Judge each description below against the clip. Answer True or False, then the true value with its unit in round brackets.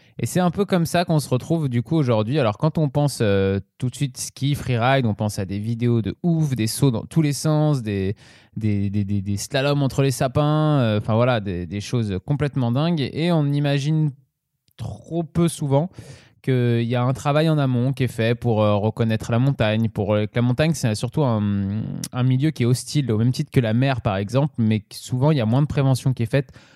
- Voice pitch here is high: False (125 Hz)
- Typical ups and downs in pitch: True (4.5 semitones)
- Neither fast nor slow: False (230 wpm)